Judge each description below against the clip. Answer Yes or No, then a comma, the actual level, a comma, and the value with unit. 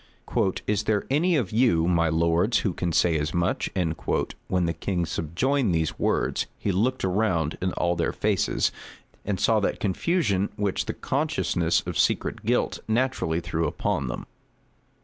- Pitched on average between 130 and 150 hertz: No, very low, 95 Hz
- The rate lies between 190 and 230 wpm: No, average, 155 wpm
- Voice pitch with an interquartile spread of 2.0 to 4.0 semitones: No, average, 4.8 semitones